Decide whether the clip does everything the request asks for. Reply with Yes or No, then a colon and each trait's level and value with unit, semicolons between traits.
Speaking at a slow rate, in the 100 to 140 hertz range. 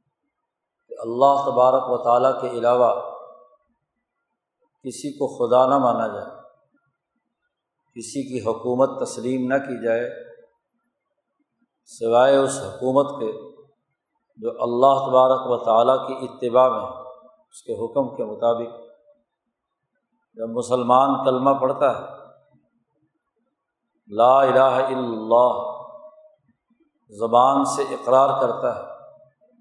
Yes: slow, 100 wpm; low, 135 Hz